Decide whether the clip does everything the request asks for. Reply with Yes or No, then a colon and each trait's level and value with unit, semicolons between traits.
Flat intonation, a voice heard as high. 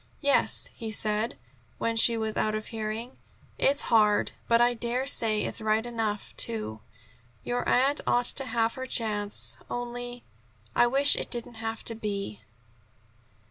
Yes: narrow, 2.1 semitones; high, 230 Hz